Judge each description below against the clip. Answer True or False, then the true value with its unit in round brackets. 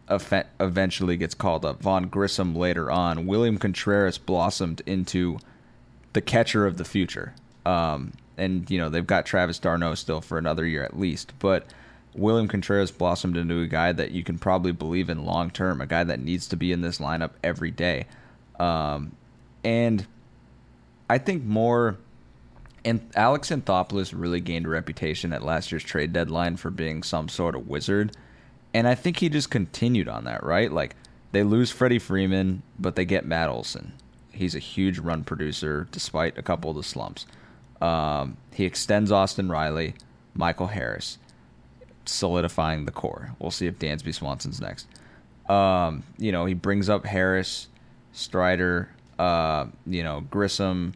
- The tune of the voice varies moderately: True (3.4 semitones)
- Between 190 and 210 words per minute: False (165 wpm)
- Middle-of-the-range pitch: False (90 Hz)